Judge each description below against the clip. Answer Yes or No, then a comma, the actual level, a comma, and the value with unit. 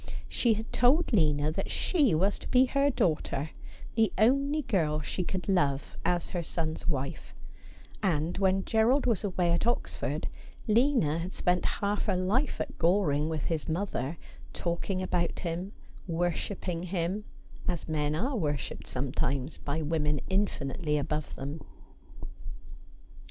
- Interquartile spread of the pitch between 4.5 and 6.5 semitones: Yes, average, 5.2 semitones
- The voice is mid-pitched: Yes, medium, 175 Hz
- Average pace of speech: Yes, average, 145 wpm